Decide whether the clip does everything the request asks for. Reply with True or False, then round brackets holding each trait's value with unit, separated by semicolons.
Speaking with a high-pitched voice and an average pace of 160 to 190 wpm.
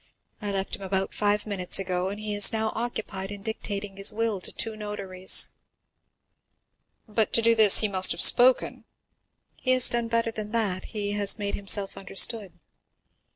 True (205 Hz; 165 wpm)